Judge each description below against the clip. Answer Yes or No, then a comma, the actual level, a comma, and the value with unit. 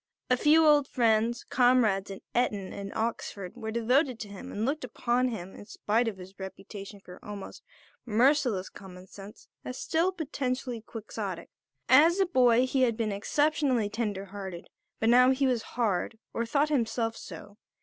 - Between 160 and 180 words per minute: Yes, average, 165 wpm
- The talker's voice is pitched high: Yes, high, 230 Hz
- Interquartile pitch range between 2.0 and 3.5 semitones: No, average, 4.1 semitones